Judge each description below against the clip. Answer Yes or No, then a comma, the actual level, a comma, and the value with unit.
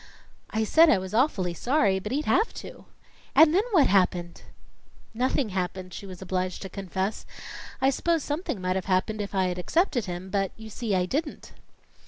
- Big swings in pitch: Yes, wide, 6.4 semitones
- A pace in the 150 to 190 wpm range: Yes, average, 180 wpm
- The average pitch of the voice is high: Yes, high, 200 Hz